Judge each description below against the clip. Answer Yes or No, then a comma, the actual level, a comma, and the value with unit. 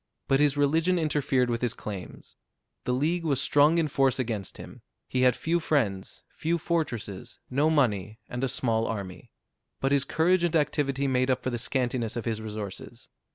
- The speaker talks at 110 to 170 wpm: No, average, 180 wpm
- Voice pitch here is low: Yes, low, 130 Hz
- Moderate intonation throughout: Yes, average, 4.5 semitones